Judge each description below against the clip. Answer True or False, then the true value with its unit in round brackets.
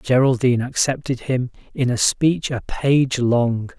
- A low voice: True (125 Hz)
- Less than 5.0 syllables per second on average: True (4.1 syllables/s)